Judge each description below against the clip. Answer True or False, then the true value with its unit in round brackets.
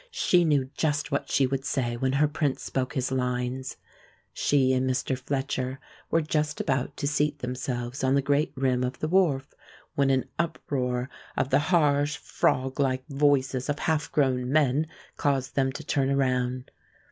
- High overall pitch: False (135 Hz)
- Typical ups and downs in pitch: False (2.1 semitones)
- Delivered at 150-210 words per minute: True (165 wpm)